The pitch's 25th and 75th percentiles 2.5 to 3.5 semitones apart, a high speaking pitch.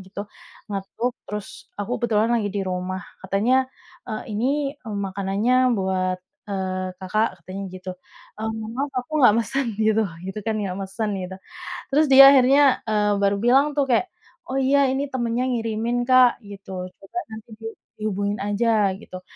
No: average, 4.0 semitones; high, 215 Hz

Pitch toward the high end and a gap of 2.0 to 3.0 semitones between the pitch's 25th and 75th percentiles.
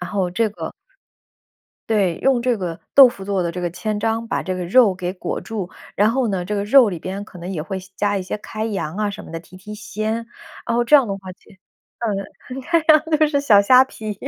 No: high, 205 Hz; average, 4.1 semitones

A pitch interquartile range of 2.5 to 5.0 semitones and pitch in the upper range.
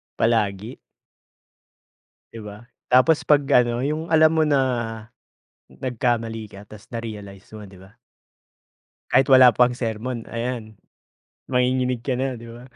No: average, 2.9 semitones; low, 120 Hz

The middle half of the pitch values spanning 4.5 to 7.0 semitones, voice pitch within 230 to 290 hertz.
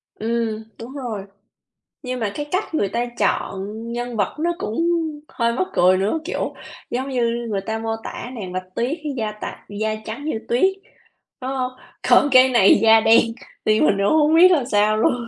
No: average, 3.4 semitones; high, 235 Hz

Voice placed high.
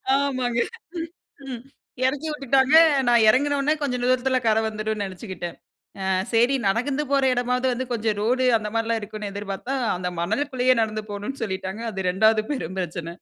Yes: high, 230 Hz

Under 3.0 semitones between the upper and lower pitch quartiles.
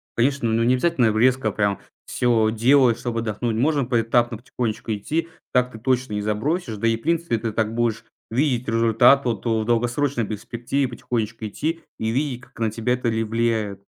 Yes: narrow, 2.4 semitones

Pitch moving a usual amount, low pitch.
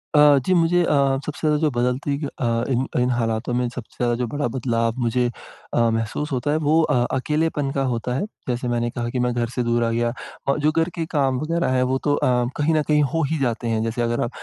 Yes: average, 3.9 semitones; low, 125 Hz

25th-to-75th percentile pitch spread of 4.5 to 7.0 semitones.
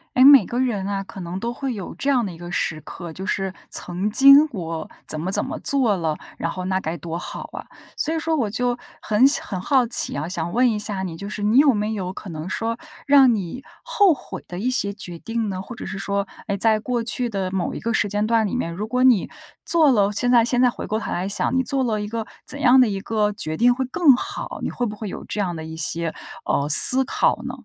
Yes: average, 5.0 semitones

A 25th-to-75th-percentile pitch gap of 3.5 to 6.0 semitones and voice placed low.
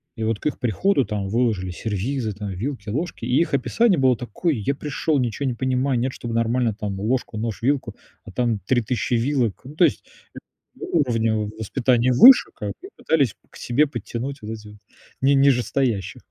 Yes: average, 3.9 semitones; low, 120 Hz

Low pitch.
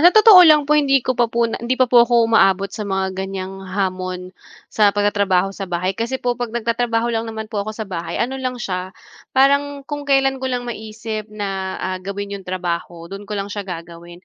No: high, 215 Hz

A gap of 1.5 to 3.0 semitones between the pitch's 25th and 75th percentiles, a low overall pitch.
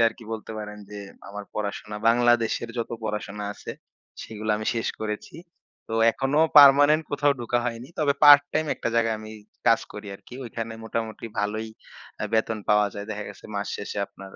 Yes: narrow, 2.4 semitones; low, 110 Hz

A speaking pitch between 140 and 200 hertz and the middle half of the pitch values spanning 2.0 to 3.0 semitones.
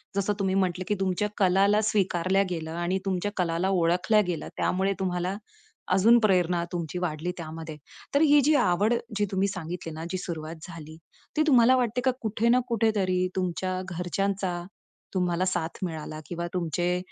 Yes: medium, 185 Hz; narrow, 2.6 semitones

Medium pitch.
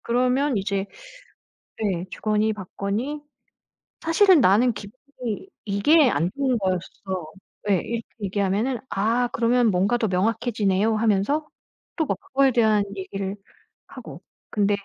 No: high, 215 Hz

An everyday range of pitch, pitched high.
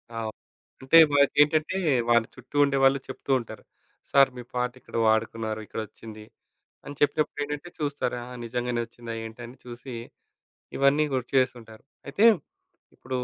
No: average, 3.4 semitones; low, 125 Hz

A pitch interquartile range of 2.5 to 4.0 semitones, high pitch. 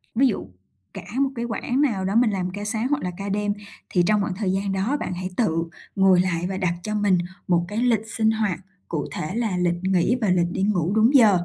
Yes: average, 3.3 semitones; high, 200 Hz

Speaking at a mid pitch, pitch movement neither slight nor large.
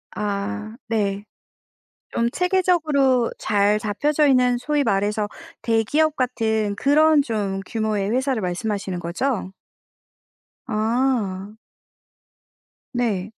No: high, 220 Hz; average, 4.6 semitones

